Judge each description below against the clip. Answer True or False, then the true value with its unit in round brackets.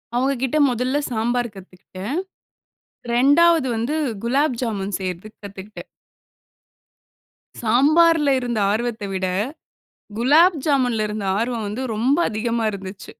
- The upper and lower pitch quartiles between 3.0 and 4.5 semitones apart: True (4.2 semitones)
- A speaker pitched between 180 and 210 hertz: False (235 Hz)